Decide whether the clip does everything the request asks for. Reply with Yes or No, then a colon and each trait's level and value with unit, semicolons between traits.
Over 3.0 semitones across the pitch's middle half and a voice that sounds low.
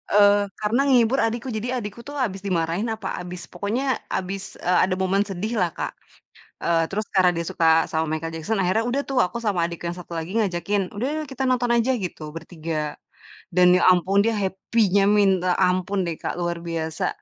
No: average, 3.8 semitones; high, 190 Hz